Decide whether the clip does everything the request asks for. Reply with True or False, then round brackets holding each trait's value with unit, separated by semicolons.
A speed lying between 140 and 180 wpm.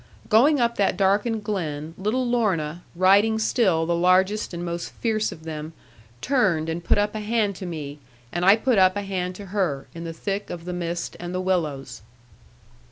False (190 wpm)